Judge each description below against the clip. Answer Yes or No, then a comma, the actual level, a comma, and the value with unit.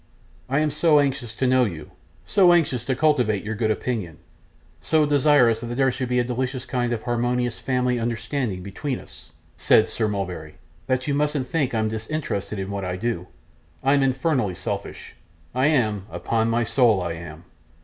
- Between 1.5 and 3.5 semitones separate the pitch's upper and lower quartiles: No, average, 4.0 semitones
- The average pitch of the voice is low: Yes, low, 120 Hz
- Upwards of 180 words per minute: No, average, 175 wpm